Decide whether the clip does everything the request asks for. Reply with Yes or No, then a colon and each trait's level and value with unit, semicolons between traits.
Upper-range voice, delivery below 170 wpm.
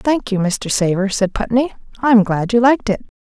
No: high, 215 Hz; fast, 205 wpm